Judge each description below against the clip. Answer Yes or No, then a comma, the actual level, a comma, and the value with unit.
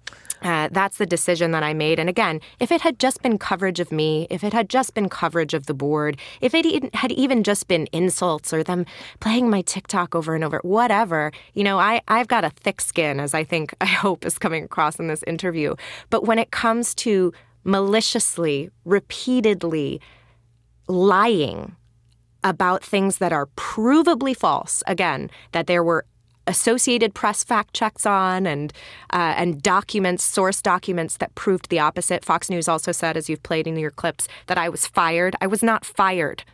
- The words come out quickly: No, average, 185 wpm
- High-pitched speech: No, medium, 180 Hz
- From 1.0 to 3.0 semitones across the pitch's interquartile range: No, average, 4.7 semitones